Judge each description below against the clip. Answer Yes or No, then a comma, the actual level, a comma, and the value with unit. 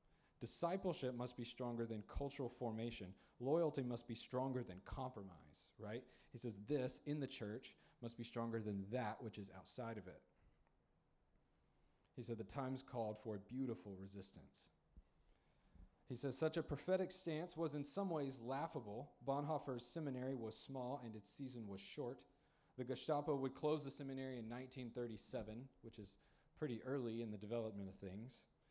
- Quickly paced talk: No, average, 160 wpm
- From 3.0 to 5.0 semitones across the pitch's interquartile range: Yes, average, 3.7 semitones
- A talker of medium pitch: No, low, 125 Hz